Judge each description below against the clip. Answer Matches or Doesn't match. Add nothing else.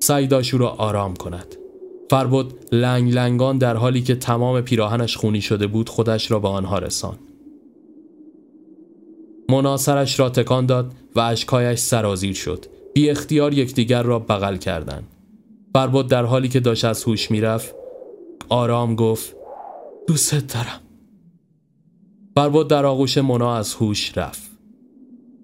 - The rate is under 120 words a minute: Doesn't match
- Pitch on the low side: Matches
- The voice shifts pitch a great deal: Matches